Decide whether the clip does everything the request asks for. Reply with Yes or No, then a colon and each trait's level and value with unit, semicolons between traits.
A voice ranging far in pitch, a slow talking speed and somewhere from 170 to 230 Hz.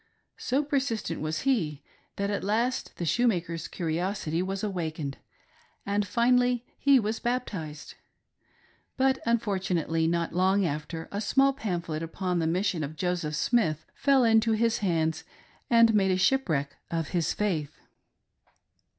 Yes: wide, 6.0 semitones; slow, 130 wpm; high, 190 Hz